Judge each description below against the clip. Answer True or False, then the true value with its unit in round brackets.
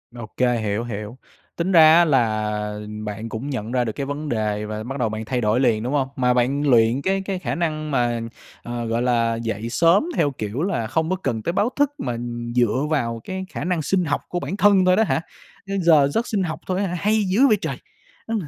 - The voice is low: True (130 Hz)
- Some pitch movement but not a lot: False (7.3 semitones)